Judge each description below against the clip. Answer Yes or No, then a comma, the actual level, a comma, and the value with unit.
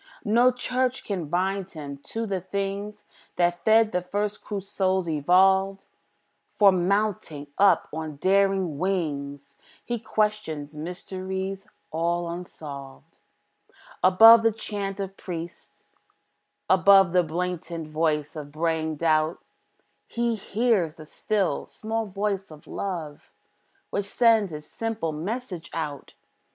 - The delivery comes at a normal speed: No, slow, 120 wpm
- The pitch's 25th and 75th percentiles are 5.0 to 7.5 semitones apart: No, average, 4.1 semitones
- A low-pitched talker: No, medium, 185 Hz